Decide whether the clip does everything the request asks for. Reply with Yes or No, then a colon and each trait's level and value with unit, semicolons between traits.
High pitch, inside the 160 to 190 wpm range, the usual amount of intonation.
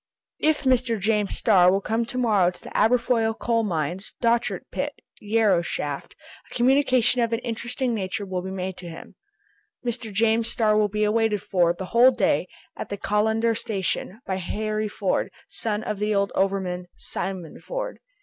Yes: high, 215 Hz; average, 170 wpm; average, 3.4 semitones